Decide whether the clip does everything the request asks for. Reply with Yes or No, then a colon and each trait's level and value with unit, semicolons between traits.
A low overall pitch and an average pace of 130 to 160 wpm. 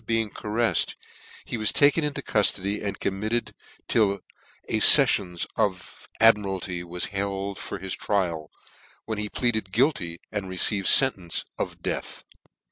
Yes: low, 100 Hz; slow, 135 wpm